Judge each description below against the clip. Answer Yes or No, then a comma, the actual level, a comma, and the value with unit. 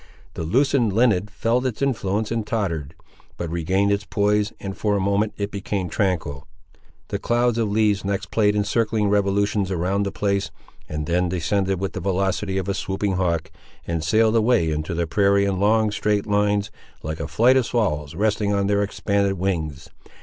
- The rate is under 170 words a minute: No, average, 180 wpm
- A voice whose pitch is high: No, low, 100 Hz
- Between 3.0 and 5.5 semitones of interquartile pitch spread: No, narrow, 2.6 semitones